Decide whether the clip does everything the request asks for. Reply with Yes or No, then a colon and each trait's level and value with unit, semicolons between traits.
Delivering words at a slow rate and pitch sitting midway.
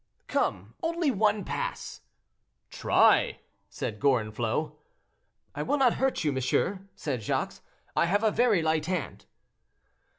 Yes: slow, 125 wpm; medium, 180 Hz